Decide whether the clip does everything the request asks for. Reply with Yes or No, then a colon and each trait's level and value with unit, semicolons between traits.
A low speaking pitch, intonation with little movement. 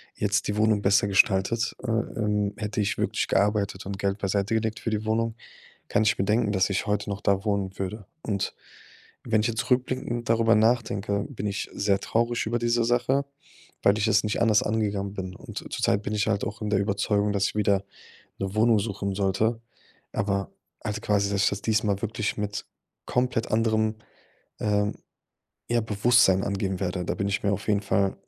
Yes: low, 105 Hz; narrow, 1.9 semitones